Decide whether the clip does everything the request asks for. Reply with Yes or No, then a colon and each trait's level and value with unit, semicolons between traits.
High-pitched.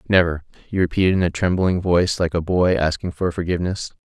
No: very low, 90 Hz